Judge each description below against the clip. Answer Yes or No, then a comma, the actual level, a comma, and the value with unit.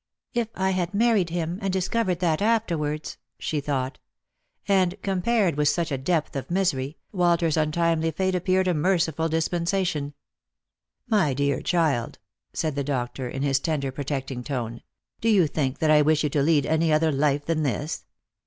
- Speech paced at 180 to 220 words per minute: No, average, 170 wpm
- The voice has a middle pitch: Yes, medium, 160 Hz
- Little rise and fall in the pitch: No, average, 4.2 semitones